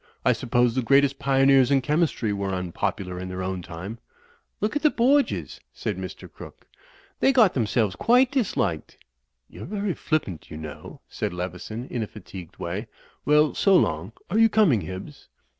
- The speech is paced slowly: No, average, 170 wpm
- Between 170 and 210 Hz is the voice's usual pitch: No, low, 125 Hz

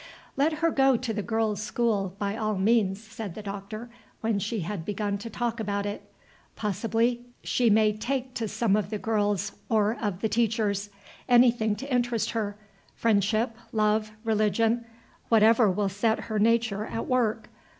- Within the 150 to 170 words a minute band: Yes, average, 160 wpm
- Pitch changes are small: Yes, narrow, 2.1 semitones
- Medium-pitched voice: No, high, 220 Hz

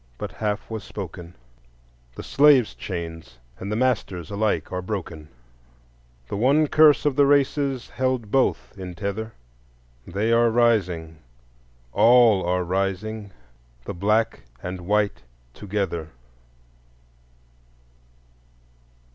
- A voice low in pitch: Yes, low, 100 Hz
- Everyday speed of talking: No, slow, 105 wpm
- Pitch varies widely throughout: No, average, 4.9 semitones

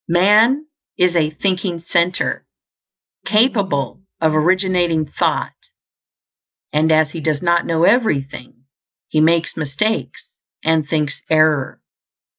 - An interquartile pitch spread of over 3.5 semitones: No, average, 3.2 semitones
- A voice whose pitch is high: No, medium, 165 Hz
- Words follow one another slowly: Yes, slow, 105 wpm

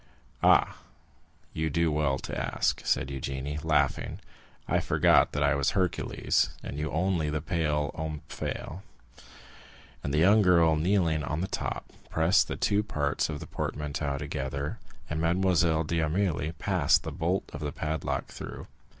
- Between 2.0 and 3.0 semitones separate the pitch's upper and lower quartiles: Yes, narrow, 2.6 semitones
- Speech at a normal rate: Yes, average, 150 wpm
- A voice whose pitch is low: Yes, very low, 80 Hz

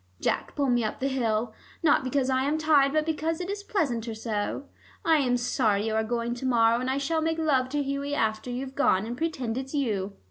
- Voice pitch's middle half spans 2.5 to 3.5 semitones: No, average, 4.2 semitones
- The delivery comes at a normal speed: No, fast, 225 wpm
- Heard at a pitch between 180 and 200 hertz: No, very high, 260 Hz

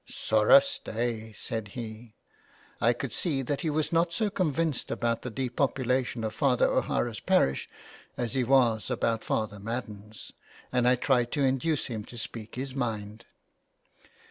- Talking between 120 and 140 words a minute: No, average, 155 wpm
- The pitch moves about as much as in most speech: Yes, average, 3.5 semitones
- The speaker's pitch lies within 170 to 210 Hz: No, low, 120 Hz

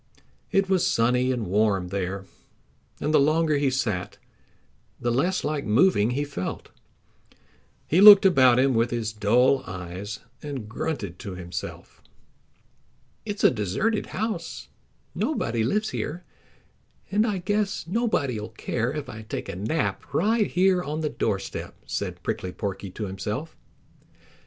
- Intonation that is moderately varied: No, wide, 8.8 semitones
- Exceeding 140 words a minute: No, slow, 135 wpm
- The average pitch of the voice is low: Yes, low, 130 Hz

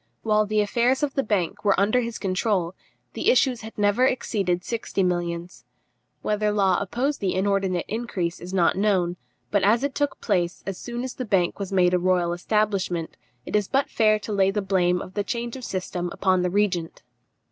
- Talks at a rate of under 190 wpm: No, average, 195 wpm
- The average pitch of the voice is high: Yes, high, 200 Hz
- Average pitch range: Yes, average, 3.5 semitones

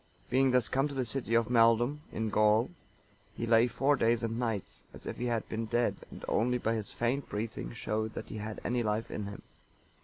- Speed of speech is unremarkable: No, fast, 215 wpm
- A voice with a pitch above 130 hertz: No, low, 115 Hz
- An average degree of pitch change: No, narrow, 2.1 semitones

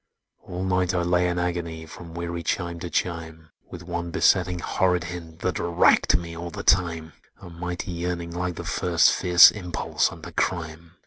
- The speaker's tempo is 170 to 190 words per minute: Yes, average, 175 wpm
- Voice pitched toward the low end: Yes, very low, 85 Hz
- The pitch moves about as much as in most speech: No, narrow, 1.0 semitones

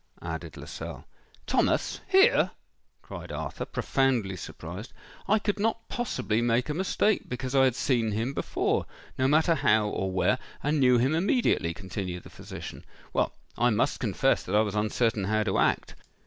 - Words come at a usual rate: Yes, average, 150 wpm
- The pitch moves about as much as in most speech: No, wide, 6.1 semitones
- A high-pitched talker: No, low, 120 Hz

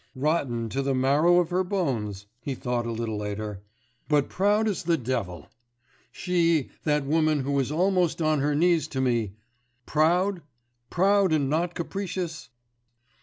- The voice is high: No, medium, 150 Hz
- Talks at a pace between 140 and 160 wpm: Yes, average, 150 wpm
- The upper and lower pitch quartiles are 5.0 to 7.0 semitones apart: Yes, wide, 5.5 semitones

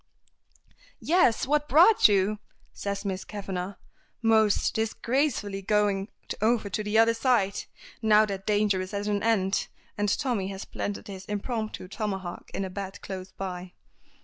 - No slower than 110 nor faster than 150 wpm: Yes, average, 145 wpm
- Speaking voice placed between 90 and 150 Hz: No, high, 205 Hz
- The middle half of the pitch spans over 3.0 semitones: No, narrow, 2.4 semitones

